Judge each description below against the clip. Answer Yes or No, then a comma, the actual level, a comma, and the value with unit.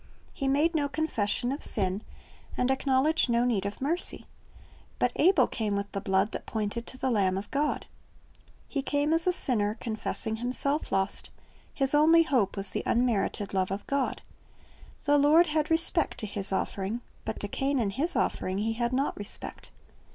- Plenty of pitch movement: Yes, wide, 6.1 semitones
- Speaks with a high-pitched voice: Yes, high, 245 Hz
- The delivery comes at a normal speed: Yes, average, 175 wpm